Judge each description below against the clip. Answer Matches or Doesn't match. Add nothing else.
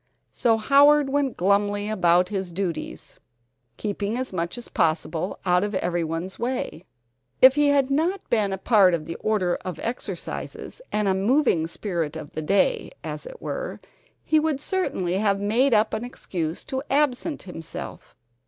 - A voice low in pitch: Doesn't match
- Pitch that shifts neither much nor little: Doesn't match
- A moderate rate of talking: Matches